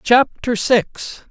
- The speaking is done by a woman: No, male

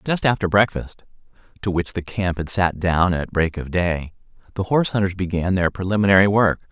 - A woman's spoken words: No, male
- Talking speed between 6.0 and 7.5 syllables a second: No, 5.4 syllables/s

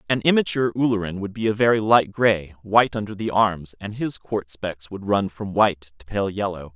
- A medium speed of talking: No, fast, 215 wpm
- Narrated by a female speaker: No, male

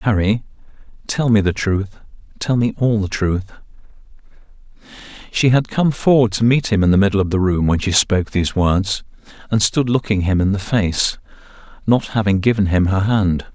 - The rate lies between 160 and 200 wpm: Yes, average, 180 wpm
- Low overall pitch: Yes, low, 105 Hz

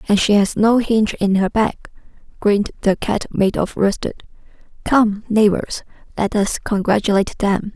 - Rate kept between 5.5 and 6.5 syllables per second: No, 4.7 syllables/s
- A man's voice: No, female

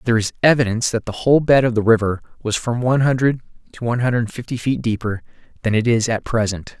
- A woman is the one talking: No, male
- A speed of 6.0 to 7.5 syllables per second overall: Yes, 6.7 syllables/s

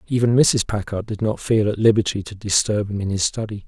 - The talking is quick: Yes, fast, 230 wpm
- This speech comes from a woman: No, male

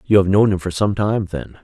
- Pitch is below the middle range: Yes, very low, 95 Hz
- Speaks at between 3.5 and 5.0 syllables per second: No, 5.3 syllables/s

